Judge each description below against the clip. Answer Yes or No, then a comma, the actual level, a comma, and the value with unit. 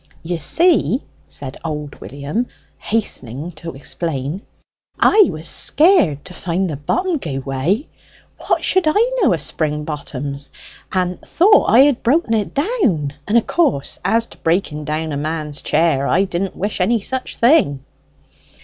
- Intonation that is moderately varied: No, wide, 8.4 semitones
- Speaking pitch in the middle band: Yes, medium, 170 Hz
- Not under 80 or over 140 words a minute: No, average, 150 wpm